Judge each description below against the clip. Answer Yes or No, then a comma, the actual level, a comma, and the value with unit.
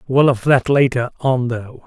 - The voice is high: No, low, 125 Hz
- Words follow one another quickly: No, average, 195 wpm